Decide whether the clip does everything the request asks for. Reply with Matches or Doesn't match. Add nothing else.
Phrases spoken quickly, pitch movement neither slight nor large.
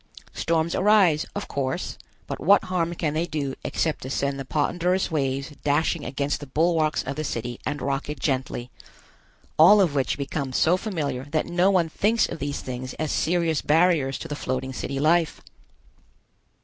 Doesn't match